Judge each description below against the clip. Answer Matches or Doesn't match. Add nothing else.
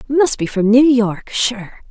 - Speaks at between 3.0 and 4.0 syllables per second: Matches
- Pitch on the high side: Matches